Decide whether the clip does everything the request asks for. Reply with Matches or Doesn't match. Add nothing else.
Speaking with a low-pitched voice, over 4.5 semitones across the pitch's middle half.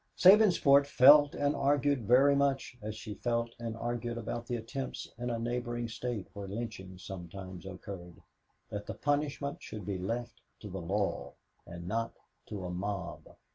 Matches